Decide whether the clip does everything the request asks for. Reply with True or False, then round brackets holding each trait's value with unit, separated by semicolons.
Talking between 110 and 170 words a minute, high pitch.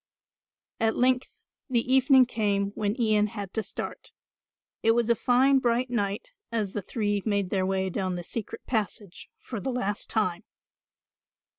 True (155 wpm; 215 Hz)